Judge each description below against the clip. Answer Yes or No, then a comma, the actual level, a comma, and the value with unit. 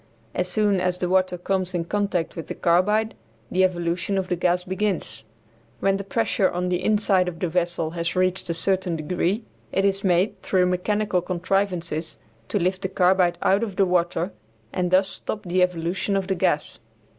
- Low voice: No, medium, 185 Hz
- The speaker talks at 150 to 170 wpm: No, average, 185 wpm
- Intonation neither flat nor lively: No, narrow, 1.9 semitones